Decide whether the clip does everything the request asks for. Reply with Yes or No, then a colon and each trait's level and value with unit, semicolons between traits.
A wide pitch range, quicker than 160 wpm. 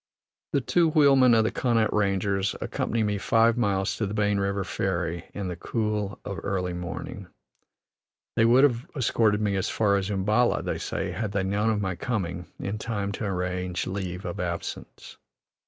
No: average, 3.0 semitones; average, 175 wpm